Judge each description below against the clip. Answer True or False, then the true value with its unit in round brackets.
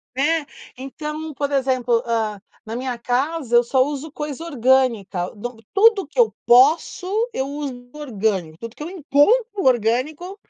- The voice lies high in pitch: True (265 Hz)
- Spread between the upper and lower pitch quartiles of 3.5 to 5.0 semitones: True (4.3 semitones)